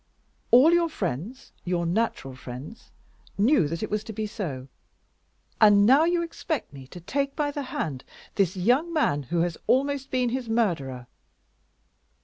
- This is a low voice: No, high, 215 Hz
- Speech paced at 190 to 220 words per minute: No, average, 155 wpm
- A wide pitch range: Yes, wide, 8.5 semitones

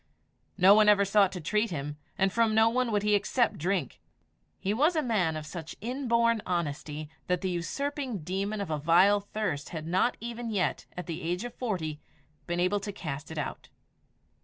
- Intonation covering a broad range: No, average, 4.8 semitones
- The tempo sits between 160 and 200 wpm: Yes, average, 190 wpm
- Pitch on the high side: Yes, high, 195 Hz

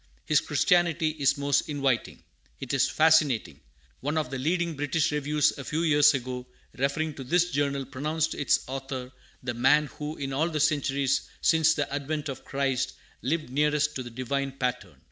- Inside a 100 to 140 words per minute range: No, average, 170 wpm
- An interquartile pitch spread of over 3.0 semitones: No, narrow, 2.4 semitones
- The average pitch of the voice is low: No, medium, 145 Hz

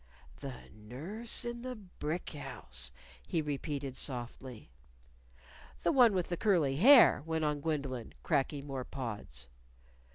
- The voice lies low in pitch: No, medium, 145 Hz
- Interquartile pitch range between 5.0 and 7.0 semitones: Yes, wide, 5.4 semitones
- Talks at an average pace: No, slow, 125 wpm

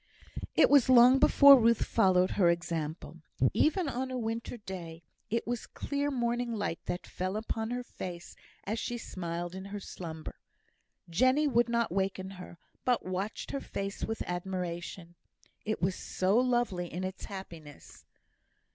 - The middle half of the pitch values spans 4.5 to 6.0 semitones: Yes, average, 5.2 semitones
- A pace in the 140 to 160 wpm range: Yes, average, 150 wpm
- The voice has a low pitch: No, high, 195 Hz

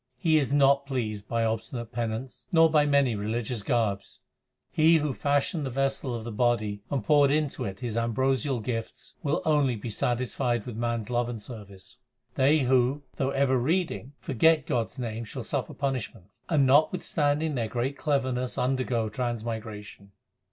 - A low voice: Yes, low, 125 Hz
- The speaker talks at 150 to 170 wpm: Yes, average, 165 wpm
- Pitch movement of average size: Yes, average, 3.6 semitones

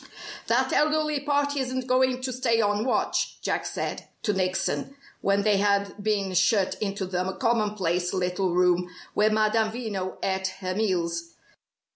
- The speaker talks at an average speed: Yes, average, 145 wpm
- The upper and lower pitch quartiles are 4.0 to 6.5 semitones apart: Yes, average, 4.4 semitones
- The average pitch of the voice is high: Yes, high, 205 Hz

